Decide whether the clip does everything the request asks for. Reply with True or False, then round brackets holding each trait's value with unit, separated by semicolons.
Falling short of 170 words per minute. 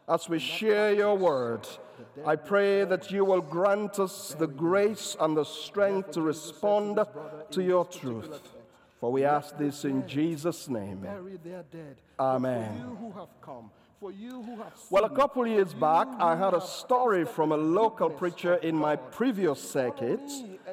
True (140 wpm)